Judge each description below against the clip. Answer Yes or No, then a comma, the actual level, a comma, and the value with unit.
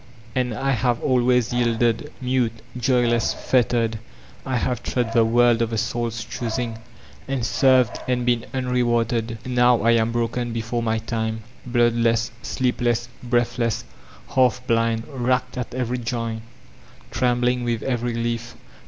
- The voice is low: Yes, low, 120 Hz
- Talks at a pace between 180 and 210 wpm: No, average, 140 wpm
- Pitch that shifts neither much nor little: No, narrow, 1.4 semitones